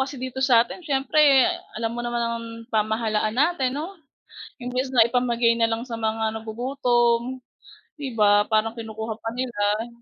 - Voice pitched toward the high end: Yes, high, 235 Hz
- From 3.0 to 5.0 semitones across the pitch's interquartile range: No, narrow, 2.4 semitones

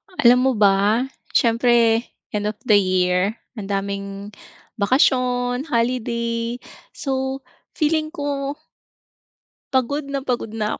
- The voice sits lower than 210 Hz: No, high, 235 Hz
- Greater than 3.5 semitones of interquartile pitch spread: Yes, average, 4.2 semitones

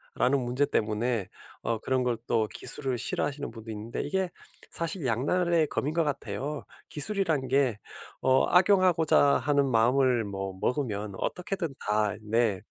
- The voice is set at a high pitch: No, low, 130 Hz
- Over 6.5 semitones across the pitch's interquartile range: No, average, 5.2 semitones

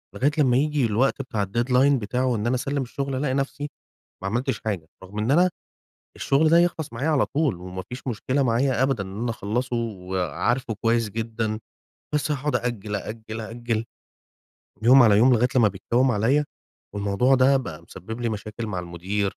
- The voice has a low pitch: Yes, low, 120 Hz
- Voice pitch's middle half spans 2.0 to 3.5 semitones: No, average, 4.1 semitones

